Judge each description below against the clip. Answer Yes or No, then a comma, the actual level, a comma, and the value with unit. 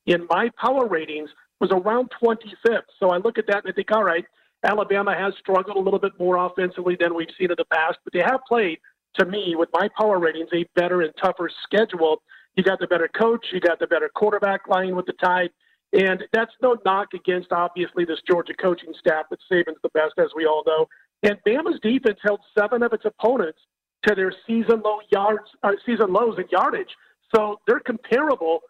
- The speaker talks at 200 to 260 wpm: Yes, fast, 205 wpm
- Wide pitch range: No, average, 3.8 semitones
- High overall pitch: Yes, high, 195 Hz